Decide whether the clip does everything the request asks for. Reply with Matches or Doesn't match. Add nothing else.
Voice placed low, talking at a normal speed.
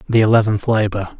Matches